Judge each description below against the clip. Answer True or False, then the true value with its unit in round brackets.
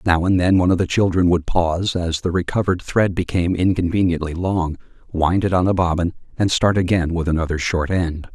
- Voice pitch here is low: True (90 Hz)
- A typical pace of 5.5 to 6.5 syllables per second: True (5.7 syllables/s)